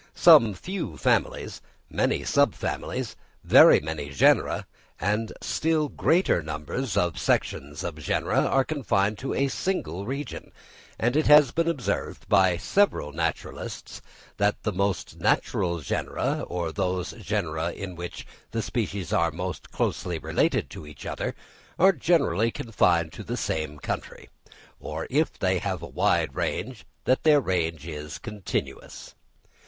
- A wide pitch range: Yes, wide, 7.7 semitones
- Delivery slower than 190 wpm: Yes, slow, 135 wpm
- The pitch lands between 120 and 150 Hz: No, very low, 95 Hz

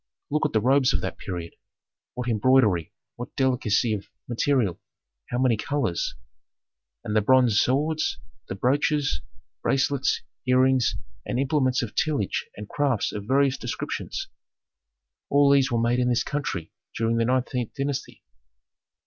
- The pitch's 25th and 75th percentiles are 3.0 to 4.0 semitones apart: Yes, average, 3.6 semitones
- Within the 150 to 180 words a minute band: No, average, 140 wpm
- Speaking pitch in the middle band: No, low, 125 Hz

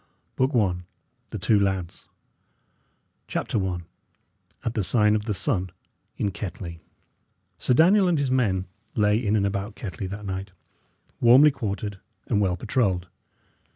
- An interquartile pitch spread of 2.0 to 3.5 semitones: No, average, 3.9 semitones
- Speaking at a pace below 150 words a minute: Yes, average, 140 wpm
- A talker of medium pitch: No, low, 105 Hz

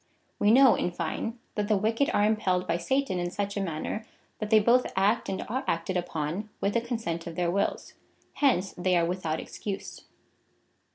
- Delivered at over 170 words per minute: Yes, average, 190 wpm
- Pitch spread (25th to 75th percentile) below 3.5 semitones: No, average, 4.0 semitones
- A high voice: Yes, high, 200 Hz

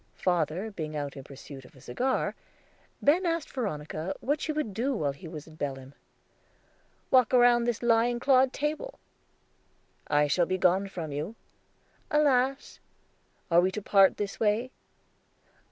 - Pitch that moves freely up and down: Yes, wide, 8.6 semitones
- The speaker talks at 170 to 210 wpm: No, average, 150 wpm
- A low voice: No, high, 200 Hz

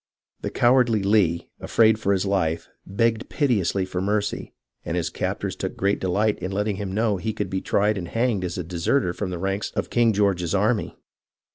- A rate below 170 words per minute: No, average, 195 wpm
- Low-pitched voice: Yes, low, 100 Hz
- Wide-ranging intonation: No, average, 2.9 semitones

